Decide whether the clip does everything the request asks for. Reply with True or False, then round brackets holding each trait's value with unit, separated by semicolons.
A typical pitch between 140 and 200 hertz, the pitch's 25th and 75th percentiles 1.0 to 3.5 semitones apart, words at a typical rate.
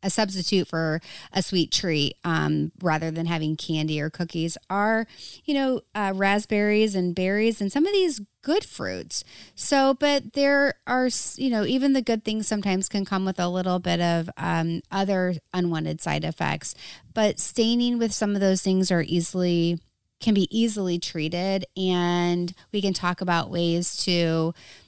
False (190 Hz; 4.2 semitones; 165 wpm)